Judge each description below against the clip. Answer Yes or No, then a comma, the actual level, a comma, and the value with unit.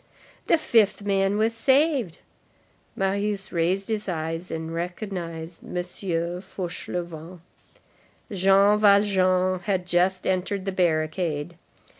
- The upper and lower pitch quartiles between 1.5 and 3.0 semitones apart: Yes, average, 2.7 semitones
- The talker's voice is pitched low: No, medium, 185 Hz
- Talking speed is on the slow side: Yes, slow, 100 wpm